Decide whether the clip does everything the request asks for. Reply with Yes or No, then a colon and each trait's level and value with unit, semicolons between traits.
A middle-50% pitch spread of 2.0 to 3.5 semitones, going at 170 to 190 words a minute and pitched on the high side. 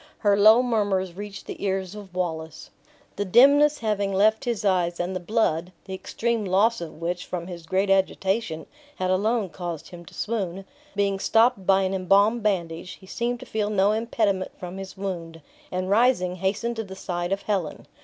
Yes: average, 2.9 semitones; average, 185 wpm; high, 195 Hz